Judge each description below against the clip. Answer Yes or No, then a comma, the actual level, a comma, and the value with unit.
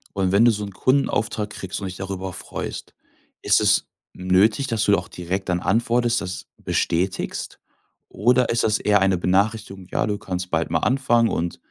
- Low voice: Yes, low, 100 Hz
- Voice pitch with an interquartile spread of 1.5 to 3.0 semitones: No, average, 3.6 semitones